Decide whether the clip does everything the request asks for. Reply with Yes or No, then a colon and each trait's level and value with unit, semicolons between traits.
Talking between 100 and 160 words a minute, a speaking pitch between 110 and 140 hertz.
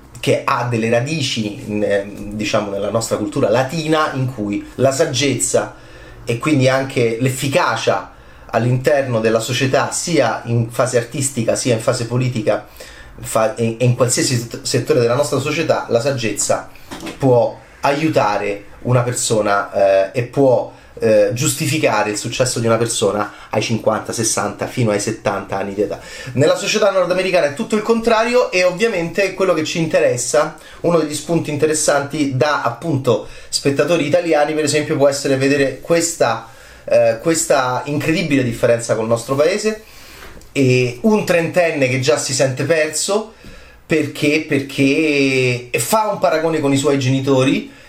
Yes: average, 140 wpm; low, 135 Hz